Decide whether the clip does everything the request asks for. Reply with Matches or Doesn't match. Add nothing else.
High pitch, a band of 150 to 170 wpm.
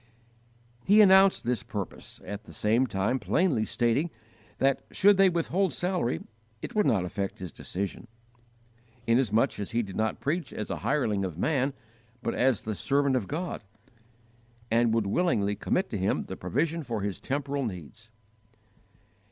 Doesn't match